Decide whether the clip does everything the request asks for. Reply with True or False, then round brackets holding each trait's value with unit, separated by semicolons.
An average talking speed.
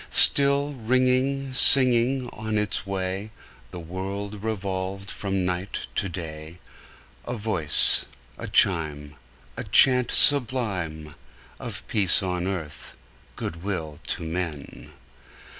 False (110 wpm)